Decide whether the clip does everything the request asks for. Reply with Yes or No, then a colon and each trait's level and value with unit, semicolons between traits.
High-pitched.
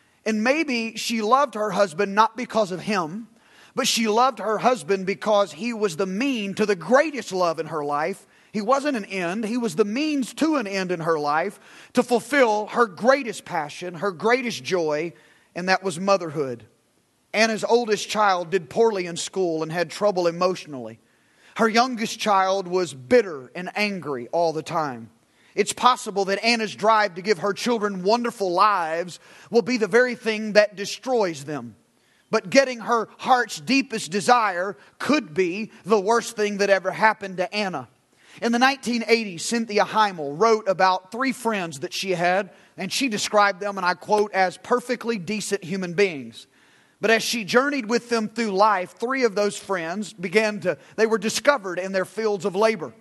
Yes: high, 210 Hz